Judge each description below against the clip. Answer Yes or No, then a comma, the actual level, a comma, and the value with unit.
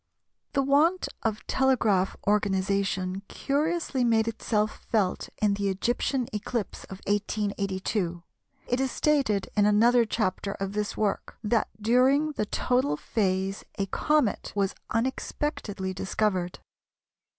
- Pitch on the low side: No, high, 210 Hz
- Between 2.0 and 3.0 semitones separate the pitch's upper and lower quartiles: No, average, 4.0 semitones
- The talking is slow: Yes, slow, 115 wpm